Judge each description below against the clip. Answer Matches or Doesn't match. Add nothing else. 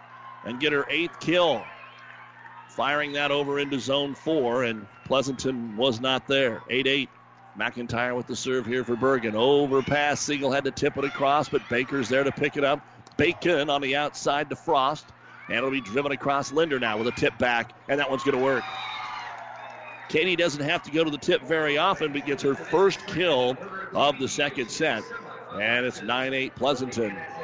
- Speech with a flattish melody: Matches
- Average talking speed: Matches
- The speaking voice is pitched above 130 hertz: Matches